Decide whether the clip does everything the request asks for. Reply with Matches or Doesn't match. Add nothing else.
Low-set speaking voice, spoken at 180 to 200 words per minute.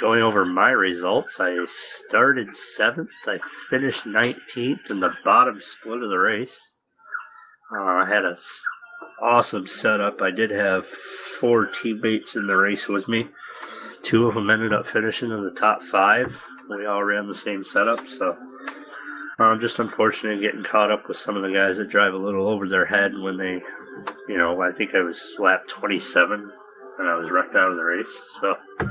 Matches